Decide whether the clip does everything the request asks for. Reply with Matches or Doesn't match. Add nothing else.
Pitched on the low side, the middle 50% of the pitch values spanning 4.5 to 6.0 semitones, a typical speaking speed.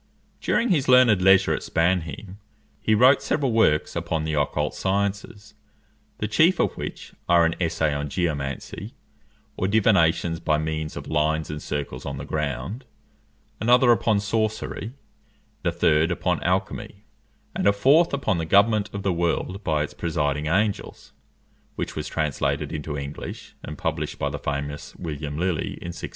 Matches